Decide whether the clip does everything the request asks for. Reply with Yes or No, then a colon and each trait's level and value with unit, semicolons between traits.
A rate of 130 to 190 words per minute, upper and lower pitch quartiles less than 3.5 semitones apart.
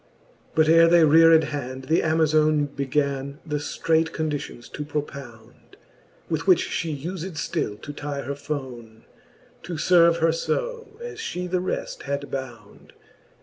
Yes: average, 145 wpm; average, 2.9 semitones